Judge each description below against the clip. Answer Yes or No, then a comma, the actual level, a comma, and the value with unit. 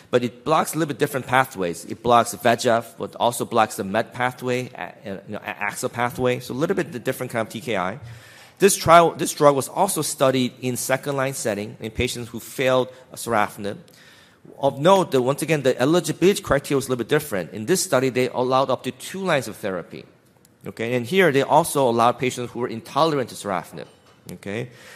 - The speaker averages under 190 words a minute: No, average, 200 wpm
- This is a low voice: Yes, low, 125 Hz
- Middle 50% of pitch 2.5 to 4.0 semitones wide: Yes, average, 3.3 semitones